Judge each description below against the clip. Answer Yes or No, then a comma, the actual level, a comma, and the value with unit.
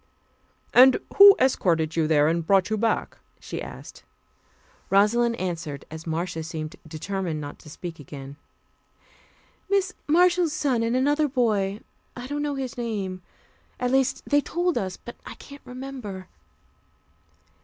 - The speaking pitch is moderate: No, high, 215 Hz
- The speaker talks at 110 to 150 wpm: Yes, average, 140 wpm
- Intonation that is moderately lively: No, wide, 8.1 semitones